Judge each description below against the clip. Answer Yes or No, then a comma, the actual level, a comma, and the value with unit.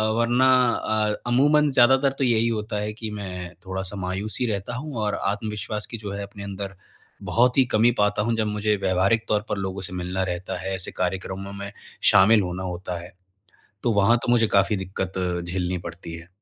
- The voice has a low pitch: Yes, low, 100 Hz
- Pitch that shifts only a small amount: No, average, 3.2 semitones